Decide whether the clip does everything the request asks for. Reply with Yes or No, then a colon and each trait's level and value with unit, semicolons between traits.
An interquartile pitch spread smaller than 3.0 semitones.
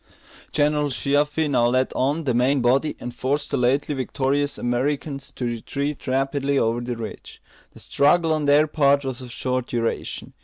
Yes: narrow, 2.6 semitones